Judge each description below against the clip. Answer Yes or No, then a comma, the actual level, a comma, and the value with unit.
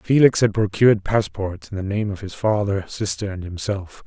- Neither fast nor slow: Yes, average, 190 wpm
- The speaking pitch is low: Yes, low, 100 Hz